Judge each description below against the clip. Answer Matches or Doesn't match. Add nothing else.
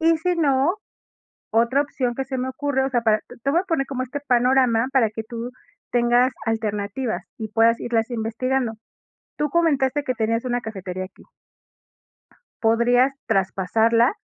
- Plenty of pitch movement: Doesn't match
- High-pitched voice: Matches